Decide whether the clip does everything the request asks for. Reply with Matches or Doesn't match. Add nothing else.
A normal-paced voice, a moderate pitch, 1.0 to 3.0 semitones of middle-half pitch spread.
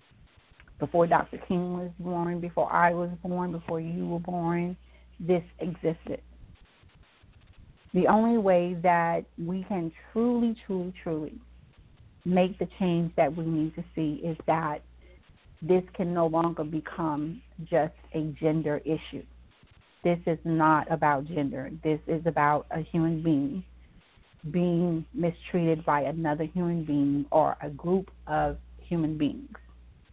Doesn't match